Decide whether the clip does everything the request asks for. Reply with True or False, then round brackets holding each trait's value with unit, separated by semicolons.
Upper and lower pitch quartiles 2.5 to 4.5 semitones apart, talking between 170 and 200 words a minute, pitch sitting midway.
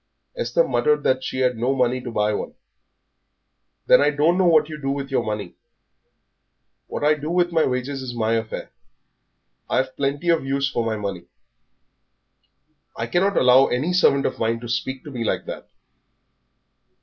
False (4.1 semitones; 175 wpm; 130 Hz)